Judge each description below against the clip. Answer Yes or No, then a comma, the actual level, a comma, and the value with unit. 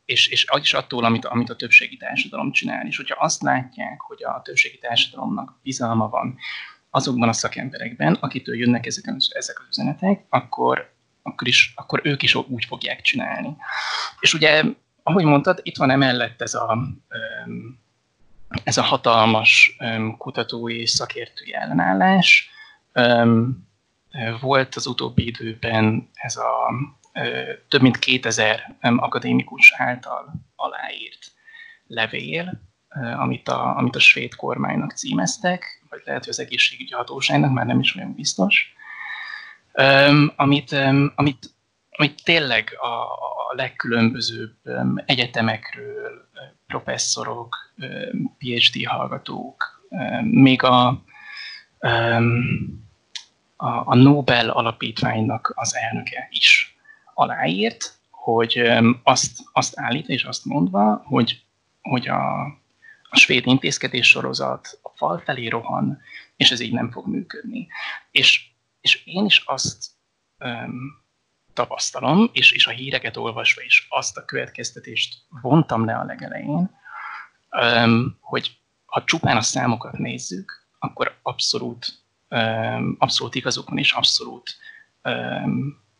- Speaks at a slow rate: No, average, 120 wpm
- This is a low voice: Yes, low, 130 Hz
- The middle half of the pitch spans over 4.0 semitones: Yes, average, 4.7 semitones